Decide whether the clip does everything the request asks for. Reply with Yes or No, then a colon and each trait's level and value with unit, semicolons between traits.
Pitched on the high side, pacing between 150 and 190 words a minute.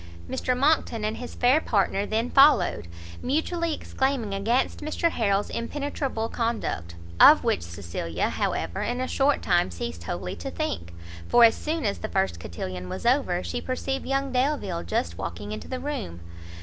Yes: high, 225 Hz; average, 160 wpm